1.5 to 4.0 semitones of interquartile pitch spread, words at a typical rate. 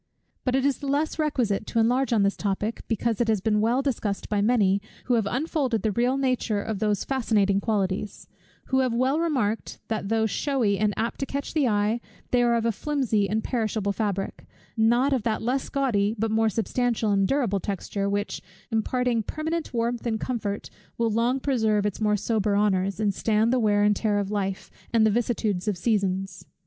Yes: average, 3.3 semitones; average, 195 wpm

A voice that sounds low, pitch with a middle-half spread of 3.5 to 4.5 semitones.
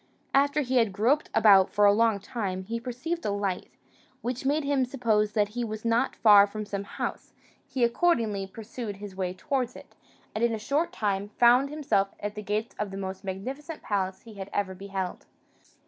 No: high, 215 Hz; average, 3.8 semitones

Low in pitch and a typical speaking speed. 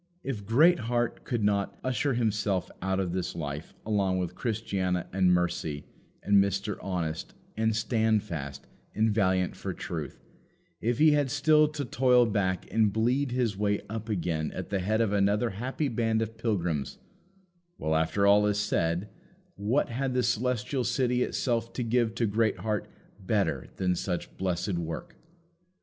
Yes: low, 105 Hz; average, 155 wpm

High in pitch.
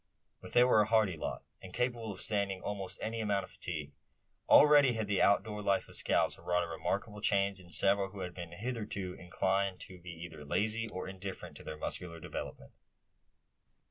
No: low, 100 Hz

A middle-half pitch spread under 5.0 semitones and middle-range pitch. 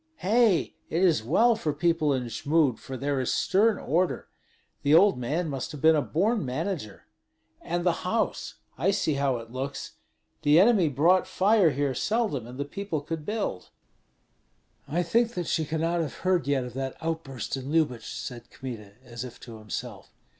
No: wide, 5.4 semitones; medium, 155 Hz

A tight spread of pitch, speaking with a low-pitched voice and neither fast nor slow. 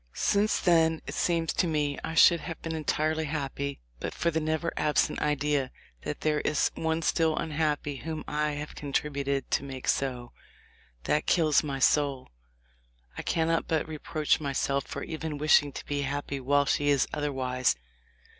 No: narrow, 2.2 semitones; medium, 150 Hz; average, 165 wpm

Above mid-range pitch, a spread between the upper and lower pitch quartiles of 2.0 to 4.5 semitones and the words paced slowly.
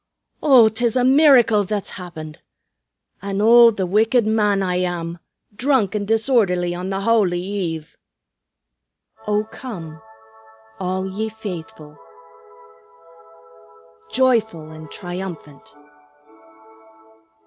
Yes: high, 200 Hz; average, 4.0 semitones; slow, 95 wpm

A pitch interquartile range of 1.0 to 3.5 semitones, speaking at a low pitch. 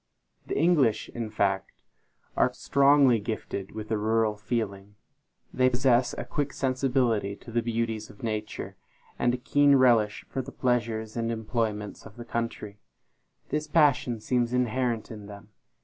Yes: average, 3.0 semitones; low, 115 Hz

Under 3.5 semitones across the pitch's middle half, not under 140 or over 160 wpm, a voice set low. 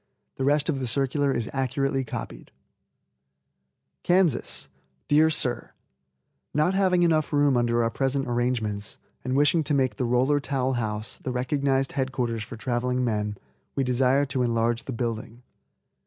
Yes: average, 3.1 semitones; average, 150 wpm; low, 130 Hz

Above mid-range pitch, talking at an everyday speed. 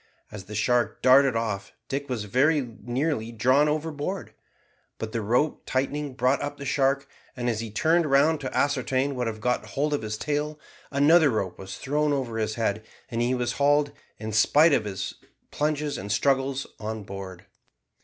No: low, 130 Hz; average, 175 wpm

